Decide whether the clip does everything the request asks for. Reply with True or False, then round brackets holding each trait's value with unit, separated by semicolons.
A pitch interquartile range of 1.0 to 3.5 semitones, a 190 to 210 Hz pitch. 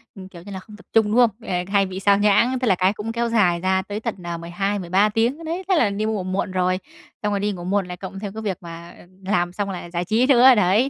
True (3.1 semitones; 200 Hz)